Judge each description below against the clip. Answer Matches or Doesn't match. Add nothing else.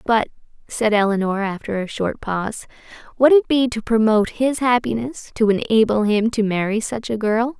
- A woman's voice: Matches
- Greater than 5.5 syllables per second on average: Doesn't match